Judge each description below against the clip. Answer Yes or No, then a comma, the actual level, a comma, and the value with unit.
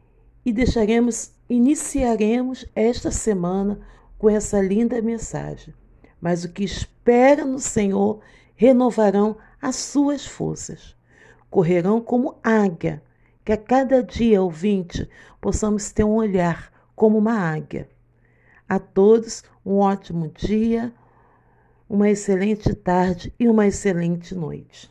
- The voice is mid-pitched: No, high, 210 Hz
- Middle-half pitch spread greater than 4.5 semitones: No, average, 3.7 semitones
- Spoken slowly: Yes, slow, 110 wpm